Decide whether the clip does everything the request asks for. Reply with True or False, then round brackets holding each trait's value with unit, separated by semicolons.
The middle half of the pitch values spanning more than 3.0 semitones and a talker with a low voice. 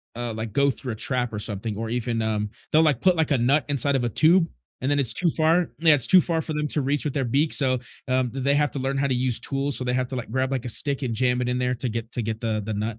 True (3.6 semitones; 130 Hz)